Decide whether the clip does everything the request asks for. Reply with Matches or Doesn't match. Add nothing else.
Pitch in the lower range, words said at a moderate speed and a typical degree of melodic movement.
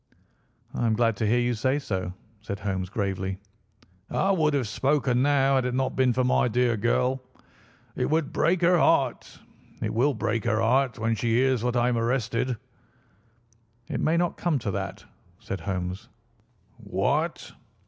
Matches